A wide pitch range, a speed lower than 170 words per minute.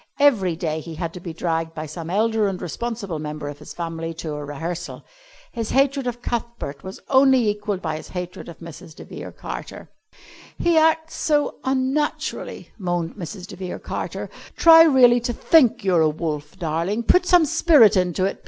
No: wide, 7.2 semitones; average, 180 wpm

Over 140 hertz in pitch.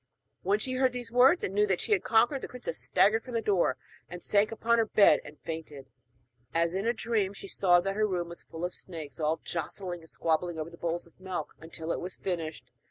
Yes: medium, 185 Hz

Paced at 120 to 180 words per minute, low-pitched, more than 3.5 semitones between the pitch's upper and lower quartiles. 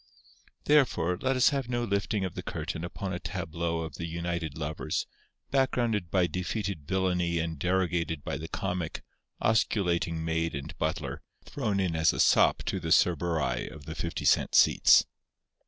No: average, 160 wpm; very low, 85 Hz; average, 3.2 semitones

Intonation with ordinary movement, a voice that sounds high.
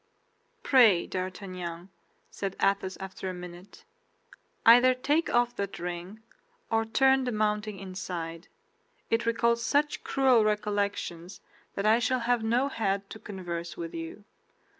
Yes: average, 4.2 semitones; high, 205 Hz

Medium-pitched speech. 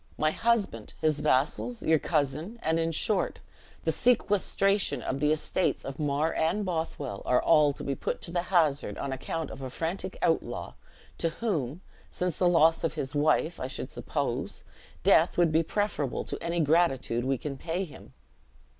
Yes: medium, 160 Hz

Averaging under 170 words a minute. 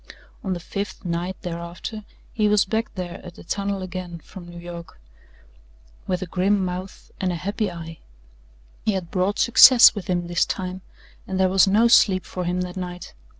No: average, 185 wpm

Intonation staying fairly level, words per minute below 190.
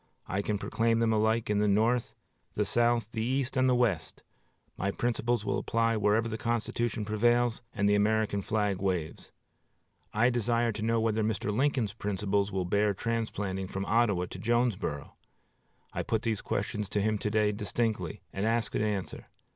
Yes: narrow, 2.3 semitones; average, 170 wpm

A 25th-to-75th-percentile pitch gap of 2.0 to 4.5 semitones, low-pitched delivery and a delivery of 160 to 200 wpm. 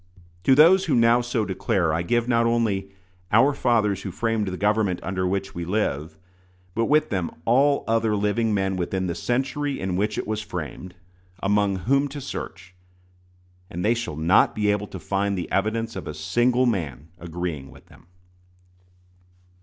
Yes: average, 4.1 semitones; low, 105 Hz; average, 170 wpm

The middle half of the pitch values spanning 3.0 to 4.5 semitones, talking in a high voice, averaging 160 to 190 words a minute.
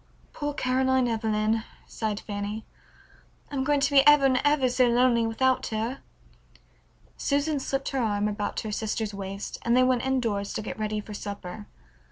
Yes: average, 3.8 semitones; high, 235 Hz; average, 165 wpm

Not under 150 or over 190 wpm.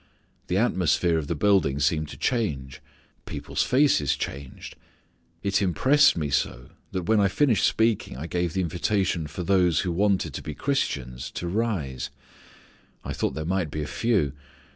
Yes: average, 165 wpm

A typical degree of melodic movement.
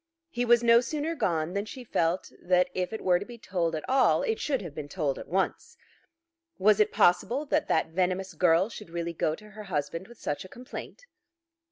No: wide, 5.8 semitones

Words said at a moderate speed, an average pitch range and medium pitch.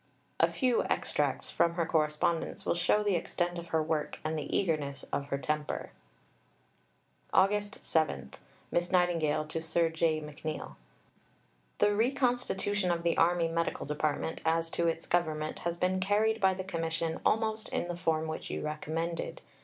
Yes: average, 155 wpm; average, 3.0 semitones; medium, 165 Hz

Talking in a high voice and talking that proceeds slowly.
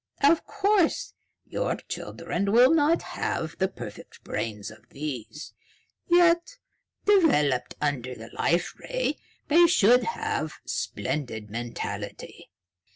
Yes: high, 200 Hz; slow, 105 wpm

